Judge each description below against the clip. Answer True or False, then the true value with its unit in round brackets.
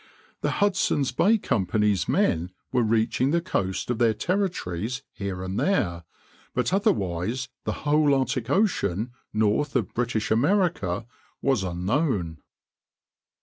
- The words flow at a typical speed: False (120 wpm)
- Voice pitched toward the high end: False (115 Hz)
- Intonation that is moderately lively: False (7.2 semitones)